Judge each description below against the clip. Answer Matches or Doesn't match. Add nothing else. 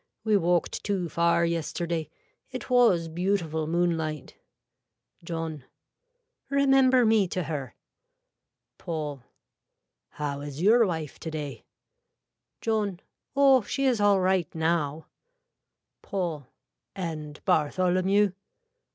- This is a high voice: Doesn't match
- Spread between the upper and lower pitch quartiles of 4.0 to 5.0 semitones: Matches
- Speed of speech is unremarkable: Doesn't match